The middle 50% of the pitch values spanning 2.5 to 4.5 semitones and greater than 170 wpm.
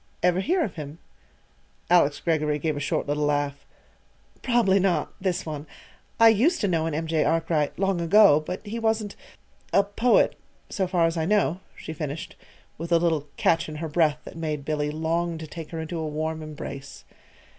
Yes: average, 3.6 semitones; average, 190 wpm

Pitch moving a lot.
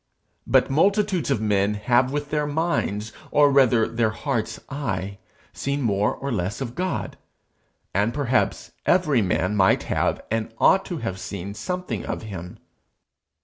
Yes: wide, 6.1 semitones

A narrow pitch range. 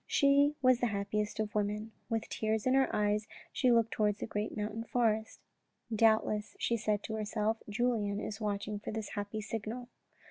Yes: narrow, 1.7 semitones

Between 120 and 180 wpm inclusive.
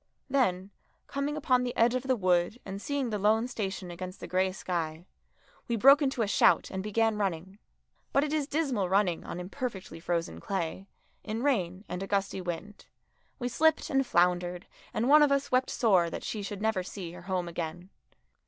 No: average, 190 wpm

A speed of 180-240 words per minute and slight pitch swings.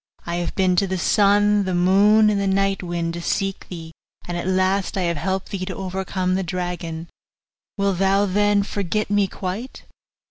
Yes: average, 185 wpm; narrow, 2.0 semitones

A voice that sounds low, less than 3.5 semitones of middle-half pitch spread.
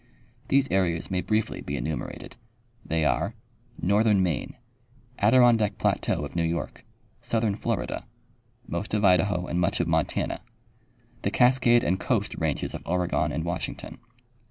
No: very low, 95 Hz; average, 4.5 semitones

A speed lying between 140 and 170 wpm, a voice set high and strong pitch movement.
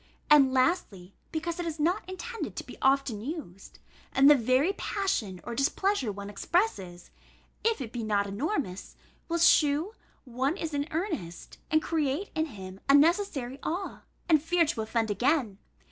Yes: average, 160 wpm; very high, 285 Hz; wide, 7.2 semitones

